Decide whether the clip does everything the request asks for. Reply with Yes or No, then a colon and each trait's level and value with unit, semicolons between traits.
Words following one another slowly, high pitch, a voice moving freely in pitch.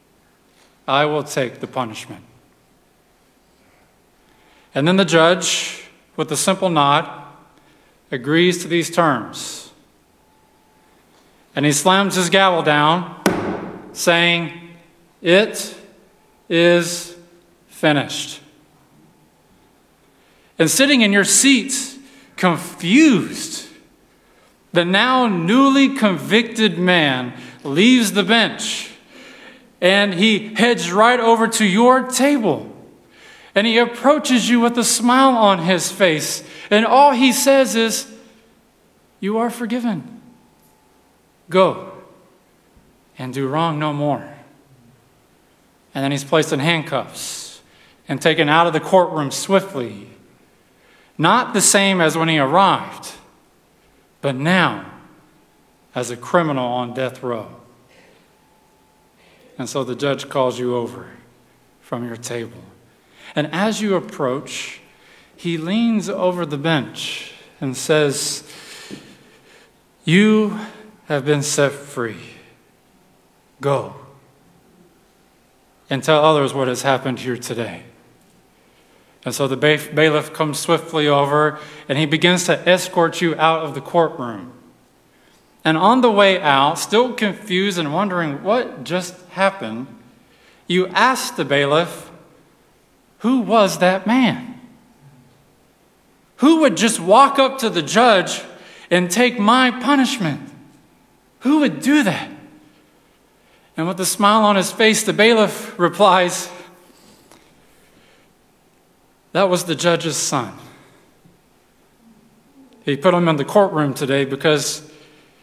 No: slow, 110 wpm; medium, 175 Hz; wide, 6.7 semitones